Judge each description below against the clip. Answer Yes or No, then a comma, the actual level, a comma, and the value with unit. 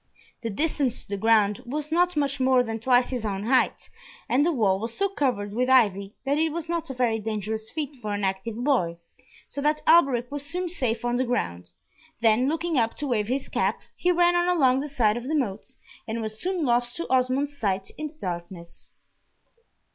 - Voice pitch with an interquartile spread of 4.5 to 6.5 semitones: Yes, average, 5.2 semitones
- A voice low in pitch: No, very high, 250 Hz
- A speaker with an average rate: No, fast, 210 wpm